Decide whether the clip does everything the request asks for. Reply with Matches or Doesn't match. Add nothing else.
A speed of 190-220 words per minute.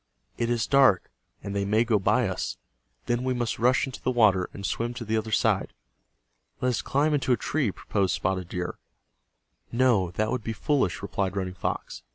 Matches